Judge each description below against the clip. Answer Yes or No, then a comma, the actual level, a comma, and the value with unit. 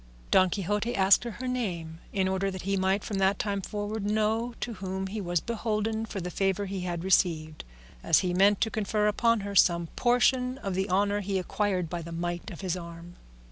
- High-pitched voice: Yes, high, 195 Hz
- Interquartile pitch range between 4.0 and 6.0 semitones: No, average, 2.8 semitones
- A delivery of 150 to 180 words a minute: No, fast, 205 wpm